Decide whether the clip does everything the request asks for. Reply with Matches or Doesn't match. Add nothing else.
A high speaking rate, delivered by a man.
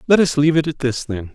Matches